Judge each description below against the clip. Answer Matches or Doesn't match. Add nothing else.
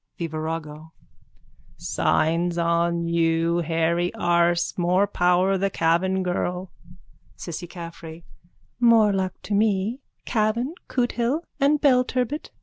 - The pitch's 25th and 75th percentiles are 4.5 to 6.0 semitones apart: Doesn't match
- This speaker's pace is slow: Matches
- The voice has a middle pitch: Matches